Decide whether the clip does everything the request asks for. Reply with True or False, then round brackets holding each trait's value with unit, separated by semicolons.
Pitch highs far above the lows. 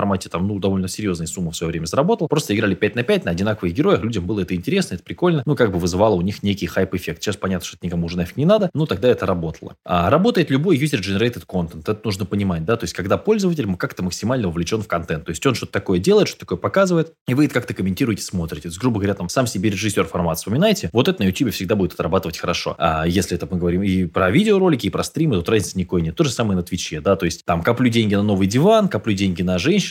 True (5.7 semitones)